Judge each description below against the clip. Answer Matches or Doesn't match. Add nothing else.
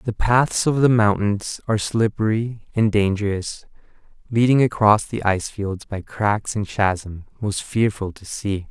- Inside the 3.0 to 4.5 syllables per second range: Matches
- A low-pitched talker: Matches